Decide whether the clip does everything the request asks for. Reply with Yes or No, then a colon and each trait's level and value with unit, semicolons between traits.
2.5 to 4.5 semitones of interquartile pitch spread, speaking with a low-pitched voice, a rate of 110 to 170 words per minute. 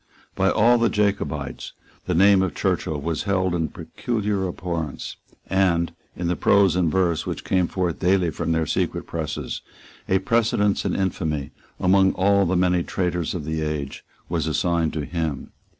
Yes: average, 3.0 semitones; very low, 90 Hz; average, 165 wpm